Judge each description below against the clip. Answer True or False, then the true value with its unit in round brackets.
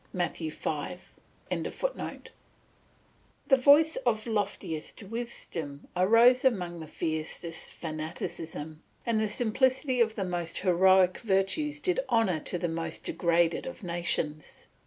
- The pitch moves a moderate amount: False (6.0 semitones)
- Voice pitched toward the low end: False (185 Hz)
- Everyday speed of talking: False (110 wpm)